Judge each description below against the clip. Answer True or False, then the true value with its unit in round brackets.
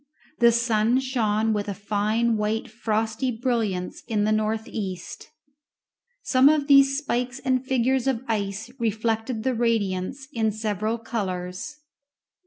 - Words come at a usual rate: False (130 wpm)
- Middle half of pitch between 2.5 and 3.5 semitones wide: True (3.0 semitones)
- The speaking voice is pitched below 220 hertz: False (225 Hz)